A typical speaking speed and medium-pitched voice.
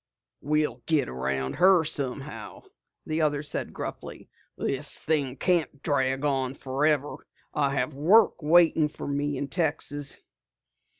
No: slow, 125 wpm; medium, 145 Hz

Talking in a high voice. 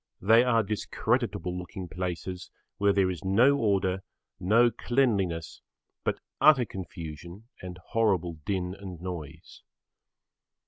No: very low, 95 Hz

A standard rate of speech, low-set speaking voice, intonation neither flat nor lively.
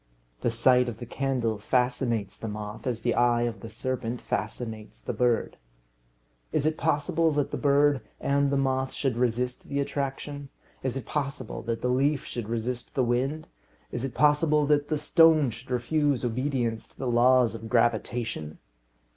Yes: average, 170 wpm; low, 125 Hz; average, 3.2 semitones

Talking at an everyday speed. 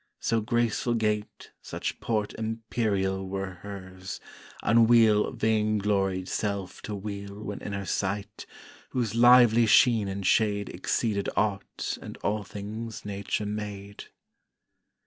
No: slow, 115 wpm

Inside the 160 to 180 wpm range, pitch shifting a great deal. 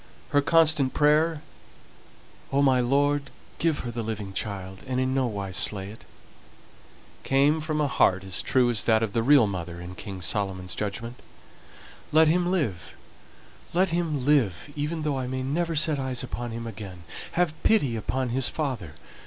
Yes: average, 170 wpm; wide, 6.2 semitones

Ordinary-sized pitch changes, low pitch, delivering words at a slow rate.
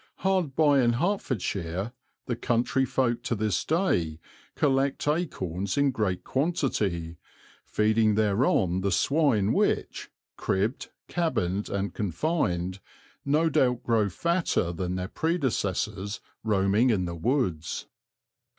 No: wide, 6.7 semitones; low, 110 Hz; slow, 115 wpm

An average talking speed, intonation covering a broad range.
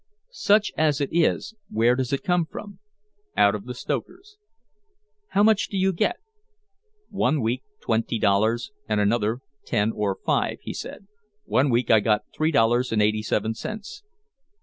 Yes: average, 160 wpm; wide, 8.1 semitones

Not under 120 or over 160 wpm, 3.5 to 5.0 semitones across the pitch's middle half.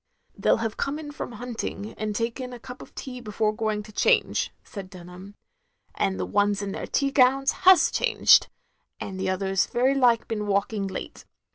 No: average, 190 wpm; average, 4.0 semitones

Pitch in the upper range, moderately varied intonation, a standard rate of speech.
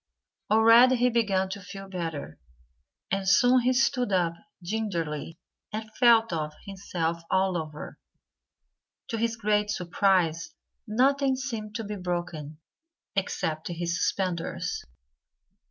No: high, 195 Hz; average, 4.9 semitones; slow, 115 wpm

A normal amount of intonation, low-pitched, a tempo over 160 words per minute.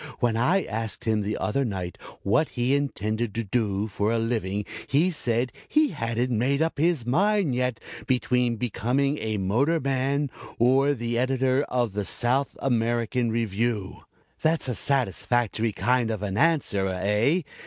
No: average, 3.9 semitones; low, 120 Hz; average, 155 wpm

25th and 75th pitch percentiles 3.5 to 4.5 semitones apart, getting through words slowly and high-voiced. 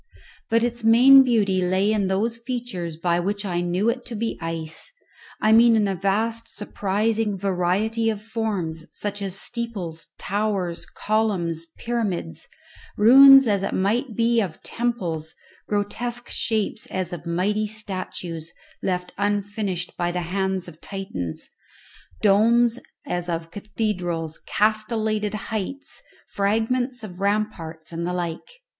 Yes: average, 4.1 semitones; slow, 130 wpm; high, 205 Hz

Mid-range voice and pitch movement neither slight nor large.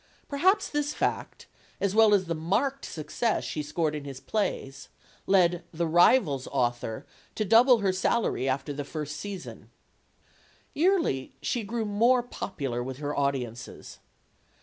No: medium, 175 Hz; wide, 8.2 semitones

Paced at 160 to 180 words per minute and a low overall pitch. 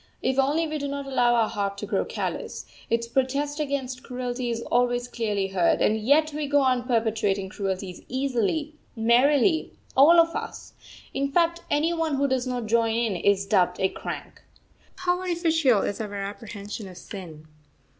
No: average, 170 wpm; high, 245 Hz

